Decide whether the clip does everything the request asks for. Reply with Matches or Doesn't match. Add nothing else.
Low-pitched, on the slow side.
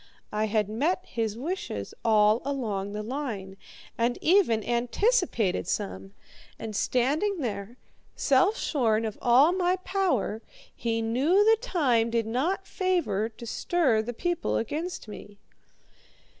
Doesn't match